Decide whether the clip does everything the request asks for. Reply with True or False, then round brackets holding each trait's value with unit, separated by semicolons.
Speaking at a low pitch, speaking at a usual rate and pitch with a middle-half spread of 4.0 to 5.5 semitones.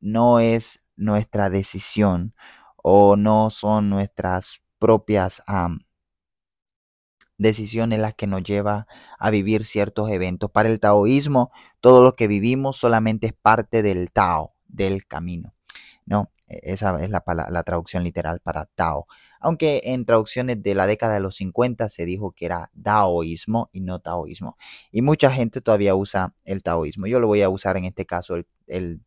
False (105 Hz; 160 wpm; 3.1 semitones)